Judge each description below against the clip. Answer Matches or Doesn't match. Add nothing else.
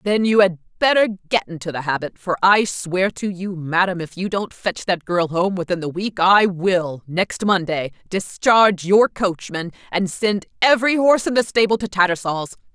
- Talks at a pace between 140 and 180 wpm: Doesn't match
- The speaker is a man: Doesn't match